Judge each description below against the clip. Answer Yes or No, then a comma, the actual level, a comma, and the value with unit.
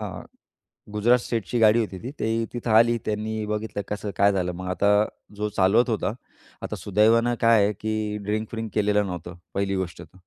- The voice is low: Yes, low, 105 Hz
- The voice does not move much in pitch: Yes, narrow, 2.0 semitones